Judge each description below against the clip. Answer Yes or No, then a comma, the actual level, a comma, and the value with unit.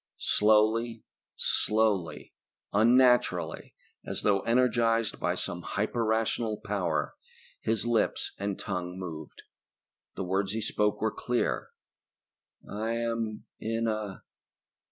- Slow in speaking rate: Yes, slow, 105 wpm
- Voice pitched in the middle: No, low, 110 Hz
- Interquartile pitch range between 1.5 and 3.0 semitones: Yes, narrow, 2.4 semitones